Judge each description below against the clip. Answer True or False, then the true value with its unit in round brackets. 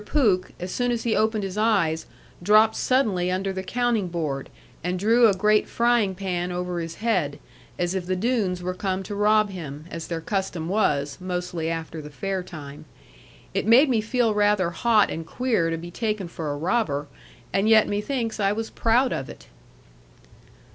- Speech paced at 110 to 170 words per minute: False (180 wpm)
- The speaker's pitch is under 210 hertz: True (190 Hz)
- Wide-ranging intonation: False (4.2 semitones)